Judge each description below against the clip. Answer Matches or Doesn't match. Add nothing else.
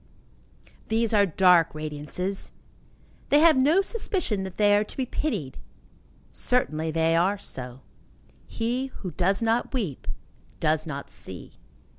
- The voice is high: Matches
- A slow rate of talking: Matches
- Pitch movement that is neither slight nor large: Doesn't match